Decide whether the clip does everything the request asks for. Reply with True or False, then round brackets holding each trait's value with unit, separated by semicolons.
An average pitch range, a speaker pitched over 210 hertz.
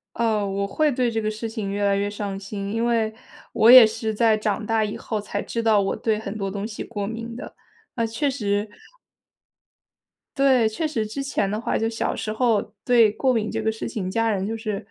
False (2.0 semitones; 220 Hz)